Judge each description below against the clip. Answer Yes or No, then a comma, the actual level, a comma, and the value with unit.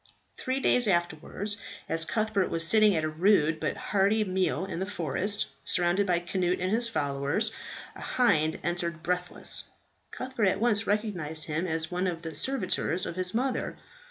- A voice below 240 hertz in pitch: Yes, medium, 185 Hz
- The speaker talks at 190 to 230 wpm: No, average, 165 wpm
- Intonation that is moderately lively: Yes, average, 4.2 semitones